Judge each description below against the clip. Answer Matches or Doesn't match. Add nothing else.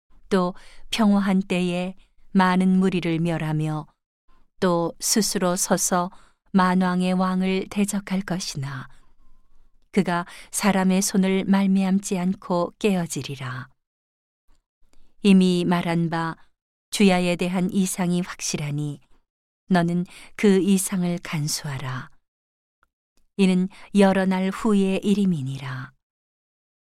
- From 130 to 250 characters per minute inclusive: Matches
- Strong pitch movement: Doesn't match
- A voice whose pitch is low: Doesn't match